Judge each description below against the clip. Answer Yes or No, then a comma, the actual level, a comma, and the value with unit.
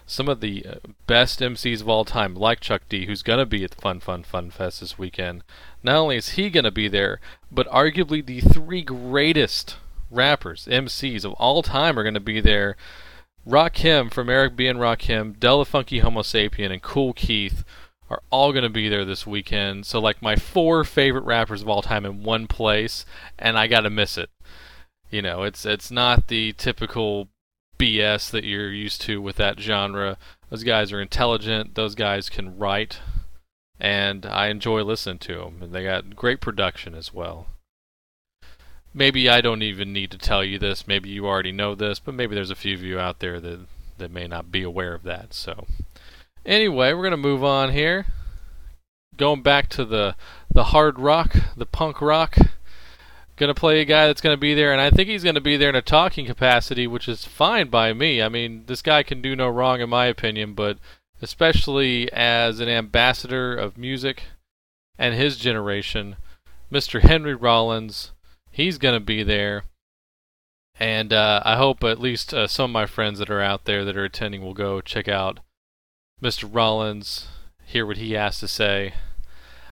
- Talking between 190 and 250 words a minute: Yes, average, 195 wpm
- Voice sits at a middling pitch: No, low, 105 Hz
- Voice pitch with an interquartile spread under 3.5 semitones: No, average, 4.6 semitones